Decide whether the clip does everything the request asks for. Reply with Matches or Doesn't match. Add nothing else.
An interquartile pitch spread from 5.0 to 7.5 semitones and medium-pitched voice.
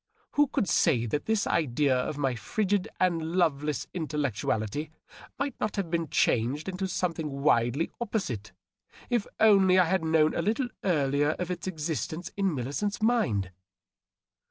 Matches